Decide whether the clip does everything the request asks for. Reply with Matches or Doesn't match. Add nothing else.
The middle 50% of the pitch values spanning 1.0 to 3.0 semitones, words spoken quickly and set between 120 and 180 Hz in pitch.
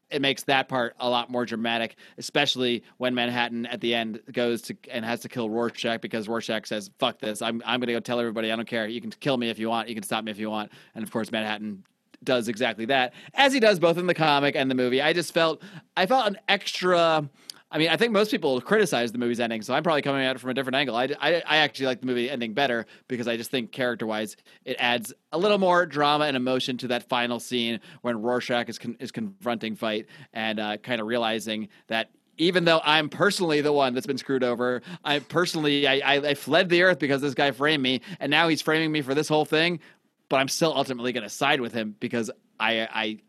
Doesn't match